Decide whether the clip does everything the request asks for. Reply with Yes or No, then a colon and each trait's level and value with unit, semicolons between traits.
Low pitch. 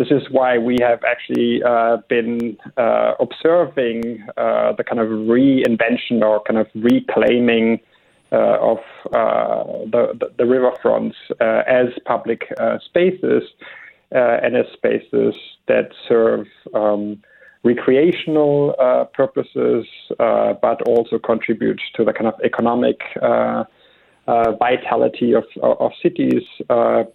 Yes: low, 115 Hz